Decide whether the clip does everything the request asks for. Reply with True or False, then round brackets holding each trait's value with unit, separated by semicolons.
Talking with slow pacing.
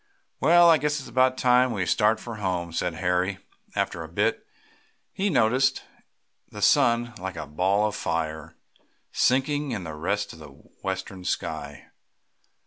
False (150 wpm)